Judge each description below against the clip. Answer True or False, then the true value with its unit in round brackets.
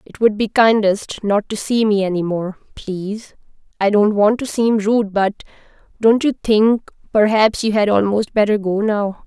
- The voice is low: False (210 Hz)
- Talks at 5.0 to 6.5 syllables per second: False (4.5 syllables/s)